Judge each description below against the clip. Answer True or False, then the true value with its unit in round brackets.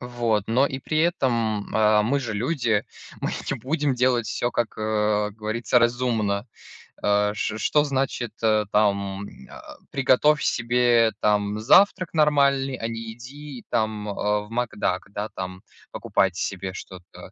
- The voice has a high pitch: False (115 Hz)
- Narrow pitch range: False (3.6 semitones)